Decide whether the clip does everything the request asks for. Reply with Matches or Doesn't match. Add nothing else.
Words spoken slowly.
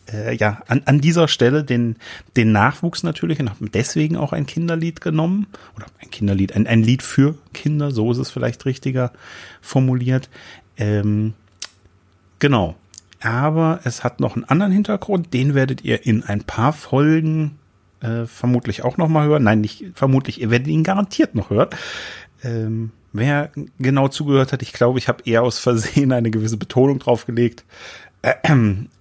Doesn't match